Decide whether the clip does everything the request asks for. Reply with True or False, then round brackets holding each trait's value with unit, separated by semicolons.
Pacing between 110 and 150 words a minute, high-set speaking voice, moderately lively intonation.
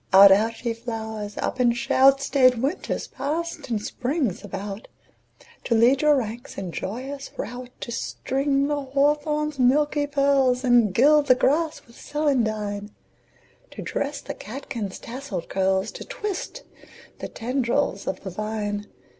True (140 wpm; 250 Hz; 4.7 semitones)